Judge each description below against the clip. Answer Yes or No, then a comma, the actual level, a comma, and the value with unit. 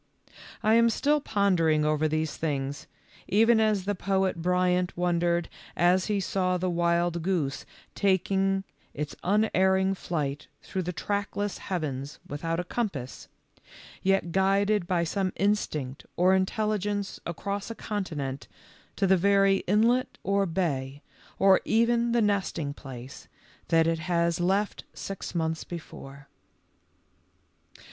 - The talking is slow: Yes, slow, 125 wpm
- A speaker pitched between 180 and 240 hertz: Yes, medium, 185 Hz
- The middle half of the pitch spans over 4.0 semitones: No, average, 3.6 semitones